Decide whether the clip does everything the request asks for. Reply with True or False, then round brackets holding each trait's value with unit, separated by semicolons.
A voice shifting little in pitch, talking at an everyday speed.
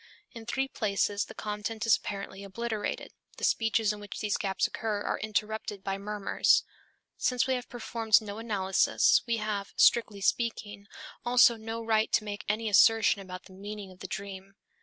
True (2.1 semitones; 170 wpm)